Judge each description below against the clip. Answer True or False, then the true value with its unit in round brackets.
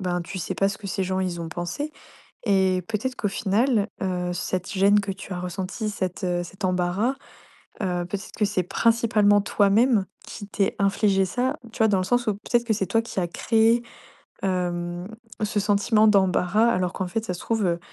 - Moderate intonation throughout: True (3.0 semitones)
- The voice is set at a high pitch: True (195 Hz)